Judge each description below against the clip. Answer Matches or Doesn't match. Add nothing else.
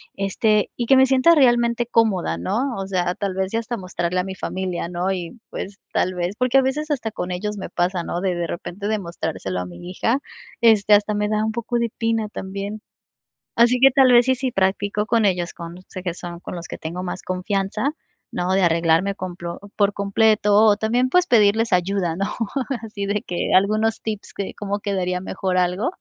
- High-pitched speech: Matches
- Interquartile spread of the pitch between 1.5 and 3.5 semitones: Doesn't match